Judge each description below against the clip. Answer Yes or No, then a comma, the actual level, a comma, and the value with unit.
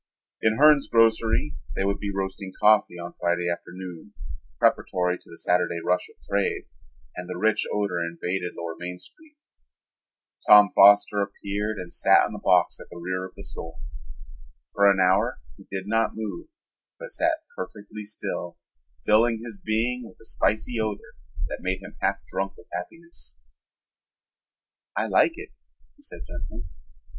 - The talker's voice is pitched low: Yes, low, 100 Hz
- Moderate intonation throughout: Yes, average, 3.6 semitones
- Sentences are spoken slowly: No, average, 155 wpm